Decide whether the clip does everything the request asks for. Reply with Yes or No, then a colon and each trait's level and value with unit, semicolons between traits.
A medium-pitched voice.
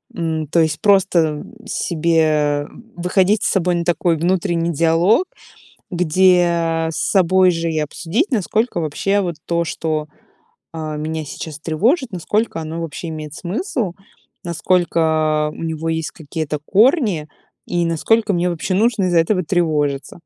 Yes: medium, 170 Hz